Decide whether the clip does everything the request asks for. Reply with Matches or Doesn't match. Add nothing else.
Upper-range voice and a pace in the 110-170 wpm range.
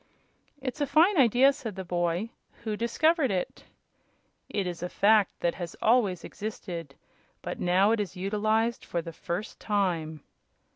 Matches